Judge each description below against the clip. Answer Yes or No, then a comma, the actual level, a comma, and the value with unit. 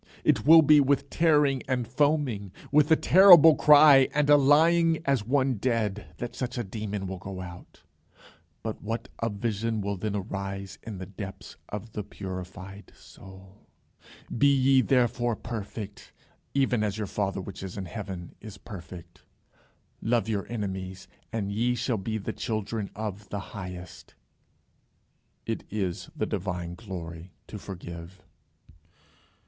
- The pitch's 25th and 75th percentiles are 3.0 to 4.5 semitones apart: No, average, 5.0 semitones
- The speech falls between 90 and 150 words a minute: Yes, average, 145 wpm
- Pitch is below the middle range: Yes, low, 105 Hz